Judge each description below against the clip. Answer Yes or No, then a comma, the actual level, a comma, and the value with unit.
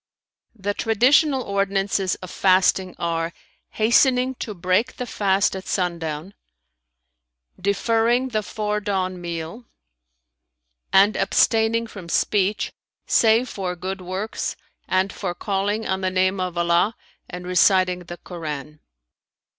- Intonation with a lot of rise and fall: No, average, 3.5 semitones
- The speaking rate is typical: No, slow, 115 wpm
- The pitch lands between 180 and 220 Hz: Yes, high, 190 Hz